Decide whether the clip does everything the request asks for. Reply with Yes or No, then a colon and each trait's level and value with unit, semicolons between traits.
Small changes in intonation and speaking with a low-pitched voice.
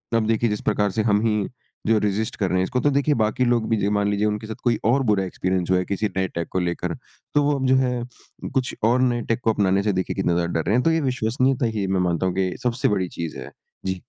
No: average, 4.4 semitones; low, 105 Hz